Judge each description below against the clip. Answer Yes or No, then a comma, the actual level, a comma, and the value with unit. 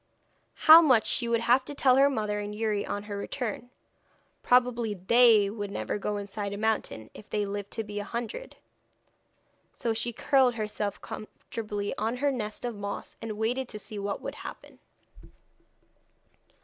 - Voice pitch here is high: Yes, high, 220 Hz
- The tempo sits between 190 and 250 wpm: No, average, 165 wpm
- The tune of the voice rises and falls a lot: No, average, 2.8 semitones